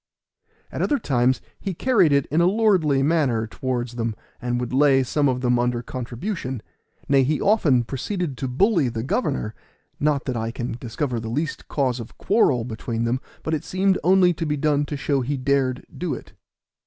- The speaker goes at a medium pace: Yes, average, 190 wpm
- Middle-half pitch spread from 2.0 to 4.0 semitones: No, average, 4.5 semitones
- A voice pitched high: No, low, 135 Hz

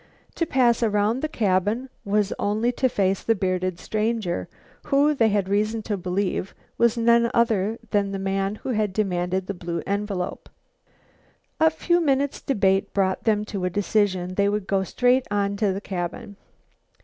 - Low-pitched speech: No, high, 205 Hz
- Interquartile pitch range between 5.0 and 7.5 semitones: No, average, 3.3 semitones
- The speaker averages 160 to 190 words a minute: Yes, average, 165 wpm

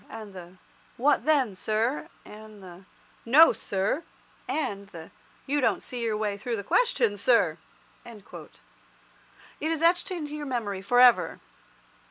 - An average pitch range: No, wide, 6.5 semitones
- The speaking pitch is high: Yes, high, 235 Hz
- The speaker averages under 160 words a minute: Yes, average, 140 wpm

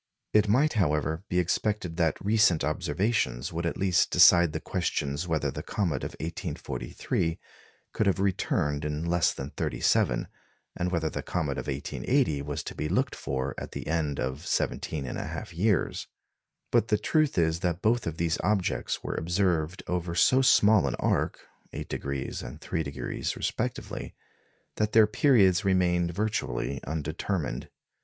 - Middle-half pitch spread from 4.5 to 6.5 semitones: Yes, average, 4.9 semitones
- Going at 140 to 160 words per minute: Yes, average, 150 wpm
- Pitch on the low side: Yes, very low, 85 Hz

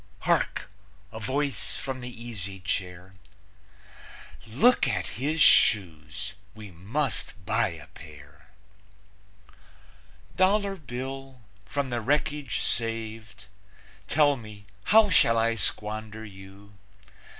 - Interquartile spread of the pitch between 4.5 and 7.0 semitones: Yes, average, 5.3 semitones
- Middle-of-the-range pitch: No, low, 115 Hz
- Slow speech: Yes, slow, 100 wpm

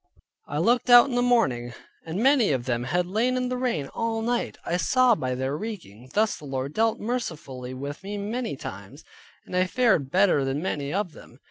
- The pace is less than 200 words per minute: No, fast, 205 wpm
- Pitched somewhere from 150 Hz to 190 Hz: Yes, medium, 185 Hz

